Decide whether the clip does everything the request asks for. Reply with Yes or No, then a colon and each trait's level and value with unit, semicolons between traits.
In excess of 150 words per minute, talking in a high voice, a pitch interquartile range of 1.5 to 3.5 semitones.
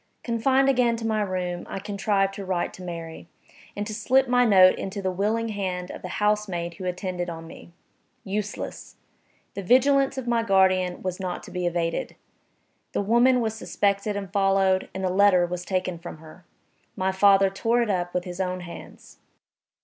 Yes: average, 180 wpm; high, 195 Hz; average, 3.0 semitones